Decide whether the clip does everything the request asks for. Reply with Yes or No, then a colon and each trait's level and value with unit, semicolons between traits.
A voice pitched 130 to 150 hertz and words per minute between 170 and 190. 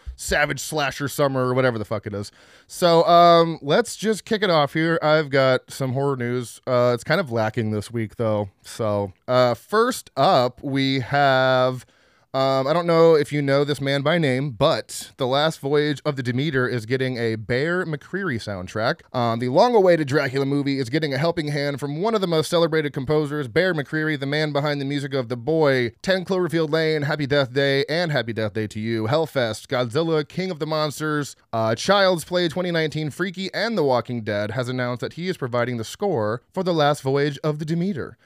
No: medium, 140 Hz; fast, 205 wpm